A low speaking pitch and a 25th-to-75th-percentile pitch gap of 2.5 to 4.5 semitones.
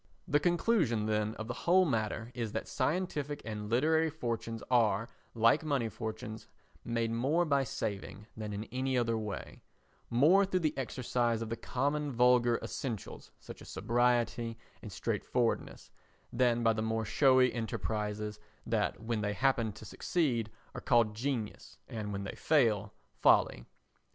Yes: low, 115 Hz; average, 3.6 semitones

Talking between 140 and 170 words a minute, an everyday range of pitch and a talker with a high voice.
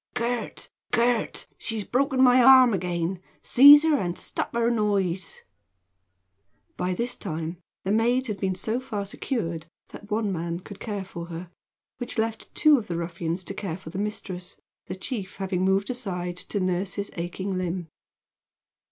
Yes: average, 160 wpm; average, 4.7 semitones; high, 195 Hz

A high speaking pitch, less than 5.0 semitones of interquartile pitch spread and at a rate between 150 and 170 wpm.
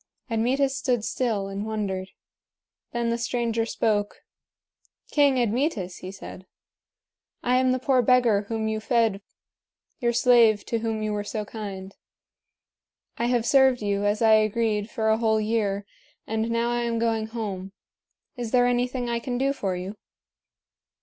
Yes: high, 225 Hz; narrow, 2.6 semitones; average, 155 wpm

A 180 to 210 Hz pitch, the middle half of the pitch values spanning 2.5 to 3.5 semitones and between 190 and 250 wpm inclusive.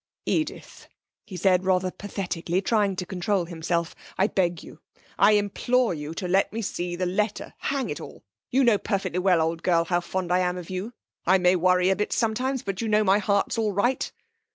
Yes: high, 190 Hz; average, 2.8 semitones; fast, 205 wpm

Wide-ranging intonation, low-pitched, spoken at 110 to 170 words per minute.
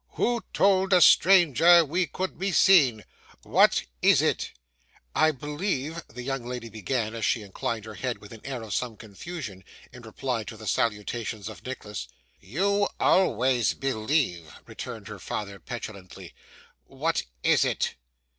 Yes: wide, 7.3 semitones; low, 125 Hz; average, 150 wpm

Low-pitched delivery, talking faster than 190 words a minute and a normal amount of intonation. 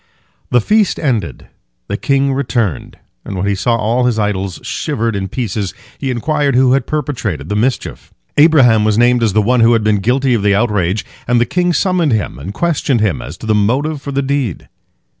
Yes: low, 120 Hz; average, 200 wpm; average, 4.8 semitones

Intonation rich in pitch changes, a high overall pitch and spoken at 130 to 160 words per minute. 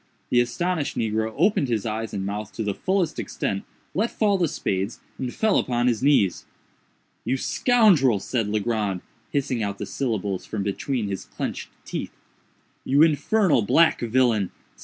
No: wide, 6.2 semitones; low, 120 Hz; average, 150 wpm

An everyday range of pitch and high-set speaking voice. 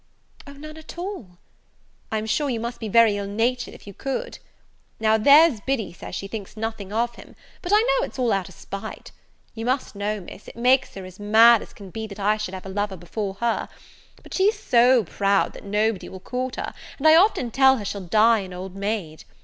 Yes: average, 4.3 semitones; high, 220 Hz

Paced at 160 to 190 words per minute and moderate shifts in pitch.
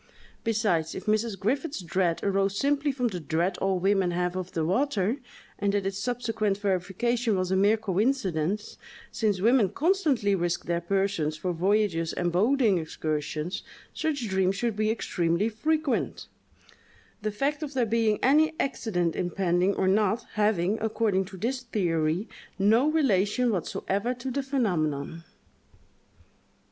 No: average, 140 wpm; average, 4.7 semitones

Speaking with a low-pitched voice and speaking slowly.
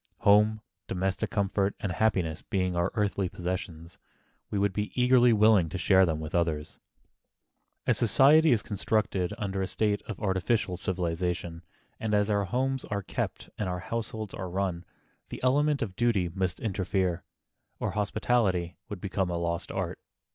No: very low, 95 Hz; average, 160 wpm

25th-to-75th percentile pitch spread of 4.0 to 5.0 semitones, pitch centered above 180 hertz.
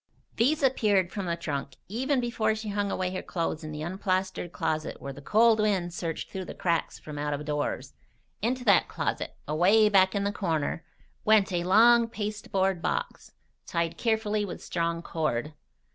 Yes: average, 4.4 semitones; high, 190 Hz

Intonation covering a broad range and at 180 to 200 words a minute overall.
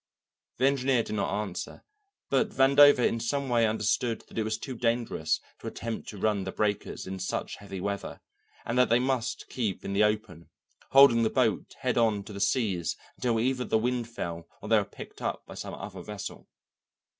No: average, 3.6 semitones; average, 195 wpm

